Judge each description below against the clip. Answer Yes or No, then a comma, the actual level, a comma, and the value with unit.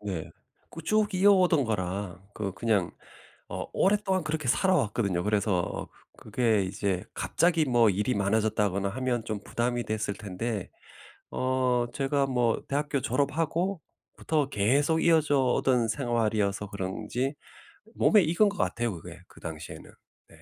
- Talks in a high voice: No, low, 120 Hz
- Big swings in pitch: Yes, wide, 6.3 semitones